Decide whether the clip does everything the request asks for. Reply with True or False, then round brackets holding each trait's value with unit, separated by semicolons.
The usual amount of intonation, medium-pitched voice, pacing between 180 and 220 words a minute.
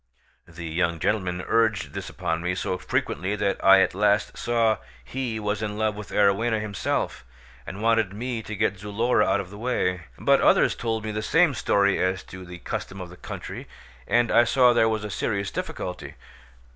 False (3.3 semitones; 105 Hz; 190 wpm)